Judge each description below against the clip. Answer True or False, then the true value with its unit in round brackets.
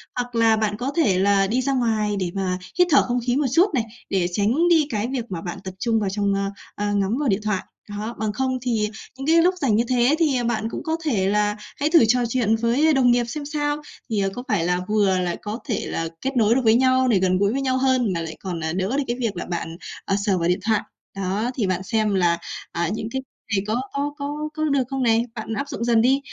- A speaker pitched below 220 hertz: False (225 Hz)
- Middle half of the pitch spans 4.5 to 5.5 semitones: True (4.9 semitones)